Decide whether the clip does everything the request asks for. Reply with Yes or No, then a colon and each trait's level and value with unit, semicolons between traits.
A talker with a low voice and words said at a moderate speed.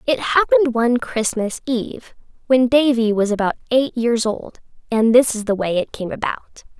No: high, 235 Hz; average, 175 wpm